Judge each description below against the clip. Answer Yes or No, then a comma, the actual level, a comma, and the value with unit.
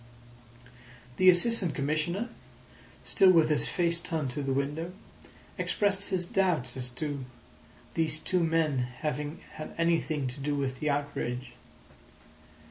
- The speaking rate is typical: No, slow, 130 wpm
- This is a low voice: No, medium, 155 Hz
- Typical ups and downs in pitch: Yes, average, 3.6 semitones